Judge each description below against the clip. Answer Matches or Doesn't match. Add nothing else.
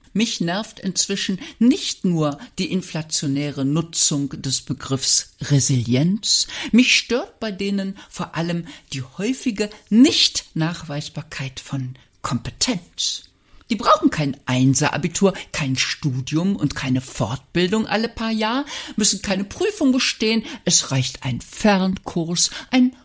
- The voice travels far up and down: Matches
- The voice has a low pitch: Doesn't match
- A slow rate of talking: Matches